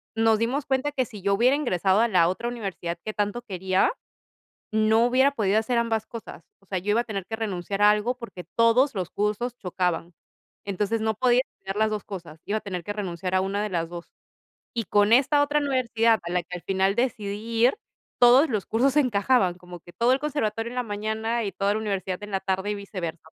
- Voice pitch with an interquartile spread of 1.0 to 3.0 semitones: No, average, 3.8 semitones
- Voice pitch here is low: No, high, 210 Hz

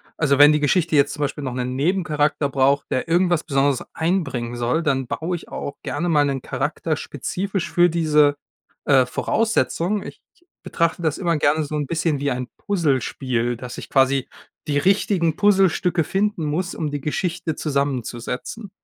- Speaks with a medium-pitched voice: Yes, medium, 150 Hz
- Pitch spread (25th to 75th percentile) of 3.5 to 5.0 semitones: Yes, average, 3.8 semitones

